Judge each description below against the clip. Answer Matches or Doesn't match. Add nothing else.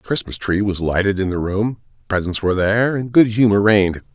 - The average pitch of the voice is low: Matches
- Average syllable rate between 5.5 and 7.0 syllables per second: Matches